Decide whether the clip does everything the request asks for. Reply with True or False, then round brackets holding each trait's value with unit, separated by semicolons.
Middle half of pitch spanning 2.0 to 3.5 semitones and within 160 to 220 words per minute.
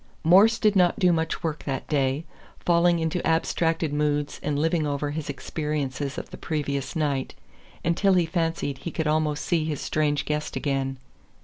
True (2.5 semitones; 170 wpm)